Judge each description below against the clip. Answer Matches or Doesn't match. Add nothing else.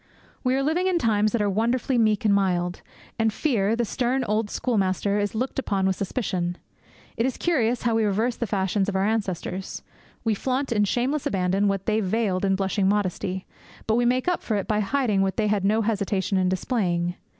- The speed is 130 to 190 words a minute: Doesn't match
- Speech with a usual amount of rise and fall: Matches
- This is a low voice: Doesn't match